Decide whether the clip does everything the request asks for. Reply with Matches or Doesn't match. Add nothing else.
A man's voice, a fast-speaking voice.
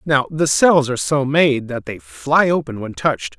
Matches